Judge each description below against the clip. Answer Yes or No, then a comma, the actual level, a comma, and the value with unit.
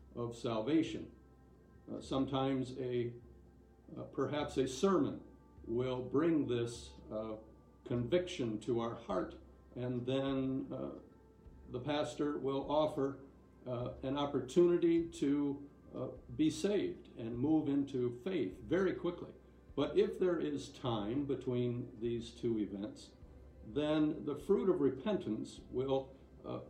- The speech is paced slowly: Yes, slow, 120 wpm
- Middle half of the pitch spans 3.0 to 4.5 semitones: Yes, average, 3.7 semitones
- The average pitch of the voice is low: Yes, low, 130 Hz